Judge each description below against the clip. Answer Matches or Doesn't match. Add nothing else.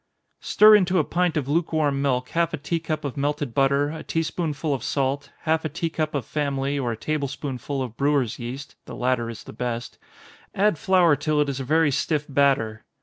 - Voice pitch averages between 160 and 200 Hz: Doesn't match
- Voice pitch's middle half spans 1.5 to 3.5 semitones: Matches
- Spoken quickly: Matches